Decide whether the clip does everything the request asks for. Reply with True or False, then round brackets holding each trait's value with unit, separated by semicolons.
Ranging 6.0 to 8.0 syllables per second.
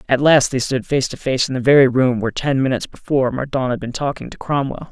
True (6.3 syllables/s)